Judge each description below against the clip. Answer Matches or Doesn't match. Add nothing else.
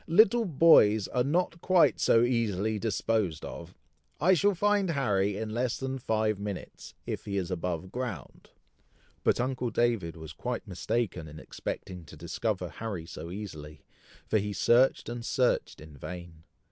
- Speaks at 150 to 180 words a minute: Matches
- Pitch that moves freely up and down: Matches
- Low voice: Matches